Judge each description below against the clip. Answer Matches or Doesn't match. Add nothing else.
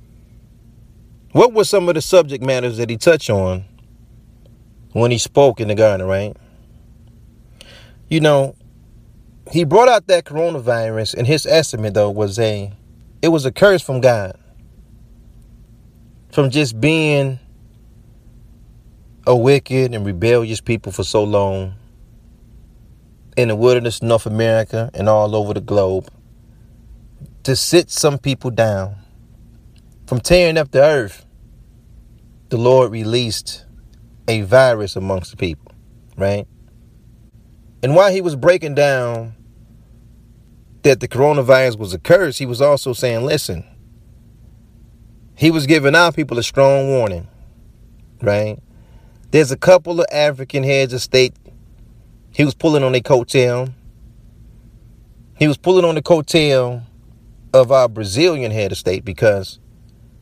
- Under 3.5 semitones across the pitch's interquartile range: Matches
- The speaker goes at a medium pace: Doesn't match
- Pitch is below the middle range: Matches